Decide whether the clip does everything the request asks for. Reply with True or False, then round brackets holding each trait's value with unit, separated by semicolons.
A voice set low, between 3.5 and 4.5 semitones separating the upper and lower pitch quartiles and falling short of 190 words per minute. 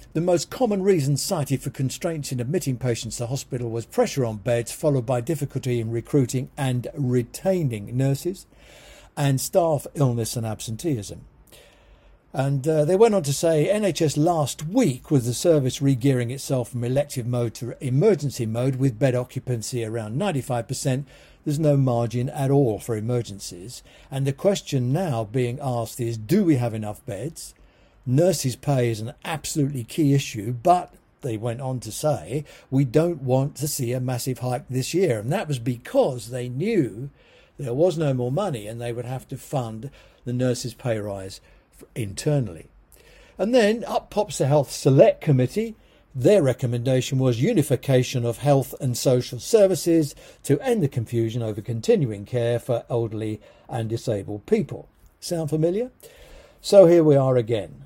True (130 Hz; 3.9 semitones; 160 wpm)